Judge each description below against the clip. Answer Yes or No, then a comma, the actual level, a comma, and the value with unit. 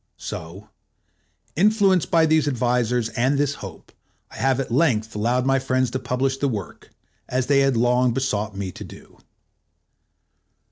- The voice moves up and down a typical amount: Yes, average, 3.2 semitones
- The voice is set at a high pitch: No, low, 125 Hz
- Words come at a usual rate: Yes, average, 150 wpm